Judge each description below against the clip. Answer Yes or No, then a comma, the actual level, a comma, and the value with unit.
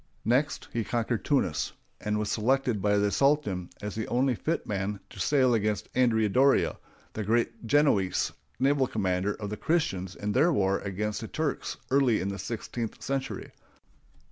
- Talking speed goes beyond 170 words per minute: No, average, 165 wpm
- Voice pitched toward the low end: Yes, low, 110 Hz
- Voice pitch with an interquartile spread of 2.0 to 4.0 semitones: No, average, 4.7 semitones